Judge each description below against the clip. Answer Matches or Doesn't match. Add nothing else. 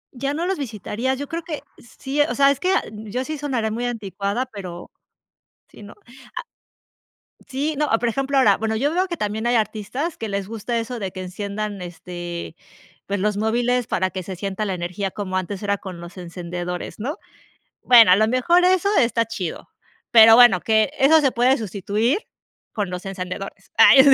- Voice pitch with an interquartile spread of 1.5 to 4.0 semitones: Doesn't match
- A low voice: Doesn't match